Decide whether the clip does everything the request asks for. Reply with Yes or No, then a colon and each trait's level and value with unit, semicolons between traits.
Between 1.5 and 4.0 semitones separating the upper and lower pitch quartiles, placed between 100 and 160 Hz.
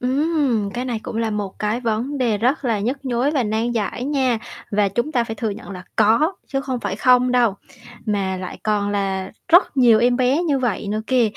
No: average, 3.7 semitones; high, 235 Hz